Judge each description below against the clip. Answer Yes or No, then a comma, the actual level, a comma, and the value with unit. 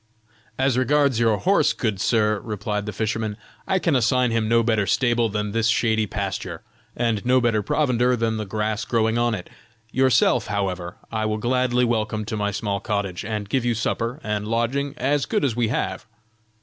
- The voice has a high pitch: No, low, 115 Hz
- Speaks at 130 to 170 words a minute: No, average, 185 wpm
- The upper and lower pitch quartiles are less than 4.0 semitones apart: Yes, narrow, 2.6 semitones